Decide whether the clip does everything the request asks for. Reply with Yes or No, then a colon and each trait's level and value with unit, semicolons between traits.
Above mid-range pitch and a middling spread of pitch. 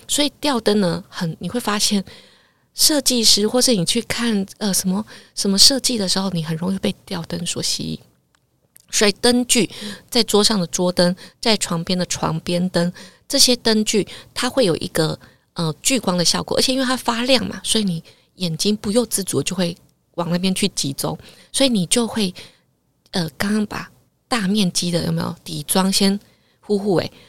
Yes: high, 200 Hz; average, 4.5 semitones